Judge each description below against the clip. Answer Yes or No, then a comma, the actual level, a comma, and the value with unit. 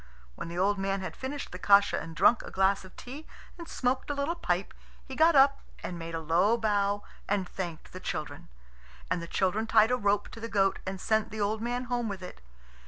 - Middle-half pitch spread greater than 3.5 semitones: Yes, average, 4.5 semitones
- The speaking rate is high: Yes, fast, 225 wpm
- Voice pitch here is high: Yes, high, 205 Hz